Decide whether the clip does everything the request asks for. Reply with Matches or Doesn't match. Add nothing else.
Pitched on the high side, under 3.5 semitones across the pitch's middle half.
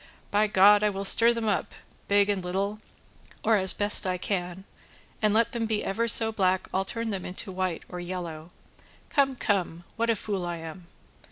Matches